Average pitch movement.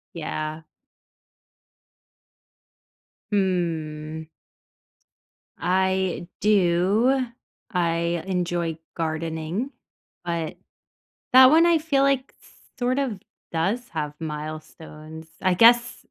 No: wide, 6.3 semitones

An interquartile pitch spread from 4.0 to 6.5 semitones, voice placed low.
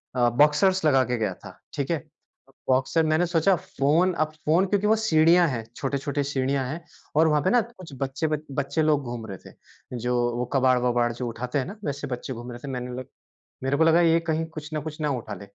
No: average, 4.4 semitones; medium, 145 Hz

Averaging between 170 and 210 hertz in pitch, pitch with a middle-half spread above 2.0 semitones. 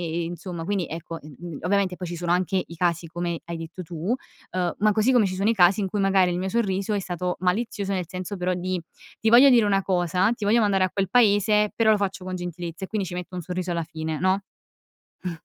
Yes: medium, 185 Hz; narrow, 2.4 semitones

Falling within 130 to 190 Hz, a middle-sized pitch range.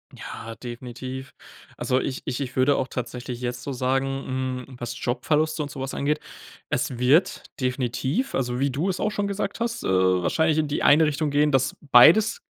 Yes: low, 135 Hz; average, 3.3 semitones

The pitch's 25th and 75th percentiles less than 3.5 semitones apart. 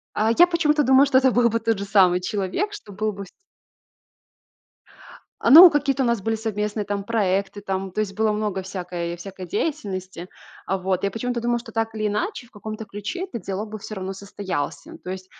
No: average, 3.8 semitones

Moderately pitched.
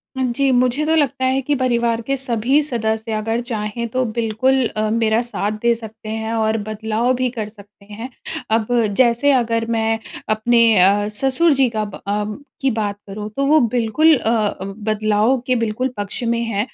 No: high, 230 Hz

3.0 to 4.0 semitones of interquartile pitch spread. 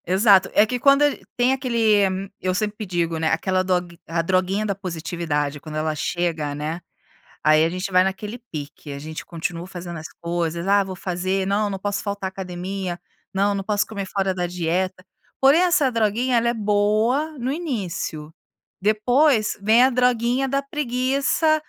No: average, 5.1 semitones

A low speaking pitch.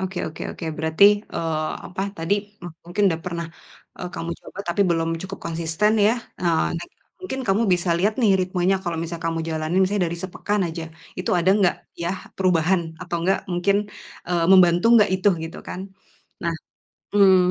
No: medium, 175 Hz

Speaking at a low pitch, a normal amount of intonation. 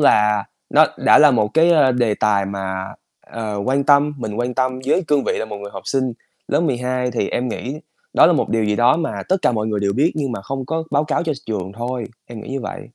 Yes: low, 125 Hz; average, 4.9 semitones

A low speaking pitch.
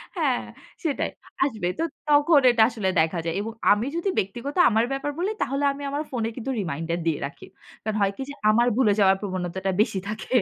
No: high, 225 Hz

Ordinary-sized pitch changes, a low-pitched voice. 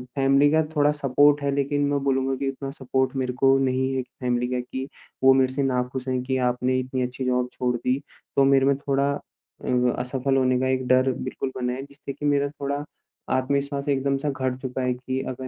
No: narrow, 1.5 semitones; low, 130 Hz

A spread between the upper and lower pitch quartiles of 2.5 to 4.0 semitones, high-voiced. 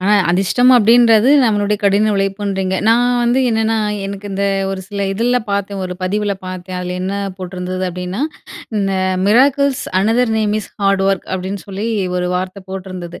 Yes: average, 2.8 semitones; high, 200 Hz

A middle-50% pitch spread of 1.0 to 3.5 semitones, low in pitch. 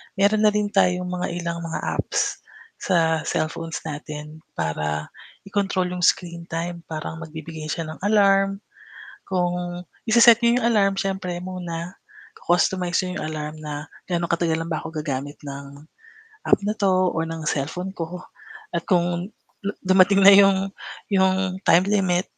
No: average, 2.9 semitones; medium, 175 Hz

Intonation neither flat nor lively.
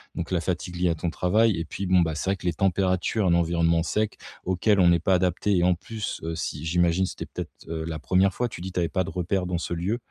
No: narrow, 2.1 semitones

